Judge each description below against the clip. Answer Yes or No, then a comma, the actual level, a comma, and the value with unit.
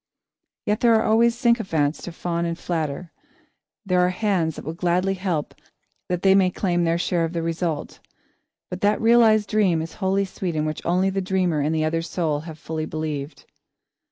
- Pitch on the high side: No, medium, 175 Hz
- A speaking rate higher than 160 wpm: Yes, average, 185 wpm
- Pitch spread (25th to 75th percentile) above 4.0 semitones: No, average, 3.2 semitones